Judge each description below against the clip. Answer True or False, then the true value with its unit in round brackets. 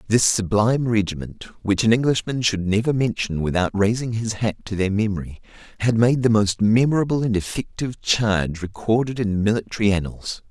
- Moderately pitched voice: False (110 Hz)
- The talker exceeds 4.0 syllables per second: True (5.5 syllables/s)